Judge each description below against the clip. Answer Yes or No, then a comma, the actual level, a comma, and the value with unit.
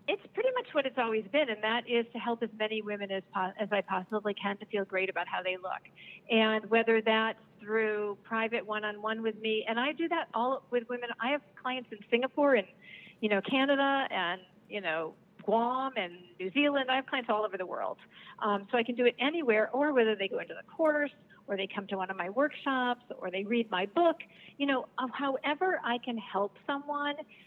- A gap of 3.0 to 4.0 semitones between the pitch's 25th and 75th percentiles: No, average, 4.5 semitones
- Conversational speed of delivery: No, fast, 215 wpm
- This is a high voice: Yes, high, 225 Hz